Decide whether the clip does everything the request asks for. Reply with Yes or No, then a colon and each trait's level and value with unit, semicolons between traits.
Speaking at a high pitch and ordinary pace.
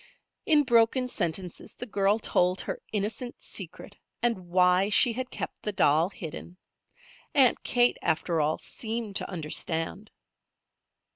No: high, 200 Hz; slow, 130 wpm